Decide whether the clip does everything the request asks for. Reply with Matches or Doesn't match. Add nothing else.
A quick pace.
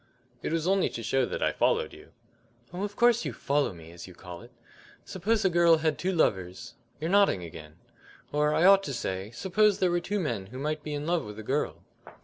Matches